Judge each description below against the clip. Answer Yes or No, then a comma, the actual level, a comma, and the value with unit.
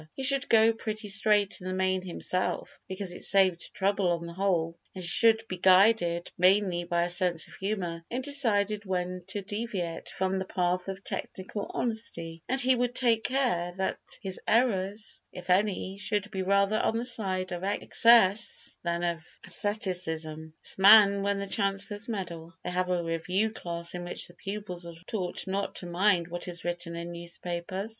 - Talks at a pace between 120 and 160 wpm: No, average, 180 wpm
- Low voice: No, high, 190 Hz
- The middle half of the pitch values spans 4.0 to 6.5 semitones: No, average, 3.1 semitones